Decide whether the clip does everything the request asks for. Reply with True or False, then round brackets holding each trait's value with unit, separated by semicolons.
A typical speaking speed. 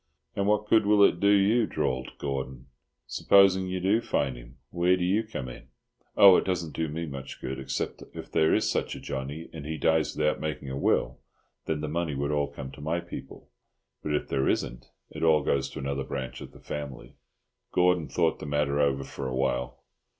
False (210 wpm)